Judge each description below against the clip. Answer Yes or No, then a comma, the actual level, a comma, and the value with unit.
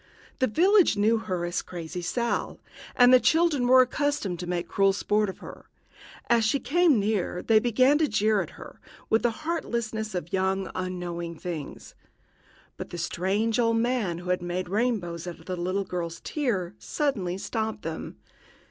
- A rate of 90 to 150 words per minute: No, average, 170 wpm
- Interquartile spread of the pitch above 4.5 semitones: Yes, average, 5.2 semitones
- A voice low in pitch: No, high, 205 Hz